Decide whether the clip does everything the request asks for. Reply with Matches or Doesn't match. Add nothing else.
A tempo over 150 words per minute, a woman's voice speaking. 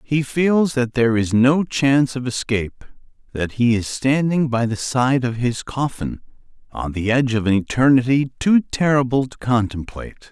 Doesn't match